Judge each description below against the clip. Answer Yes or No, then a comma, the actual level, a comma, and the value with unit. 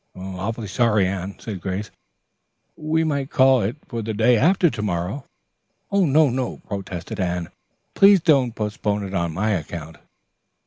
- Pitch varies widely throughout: Yes, wide, 6.0 semitones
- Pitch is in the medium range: No, low, 105 Hz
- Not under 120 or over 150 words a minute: Yes, average, 145 wpm